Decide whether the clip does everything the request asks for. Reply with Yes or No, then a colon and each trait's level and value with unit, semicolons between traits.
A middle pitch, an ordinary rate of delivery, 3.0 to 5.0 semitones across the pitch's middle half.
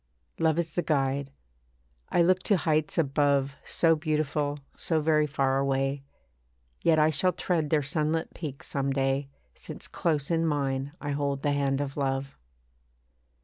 No: medium, 145 Hz; average, 150 wpm; narrow, 2.4 semitones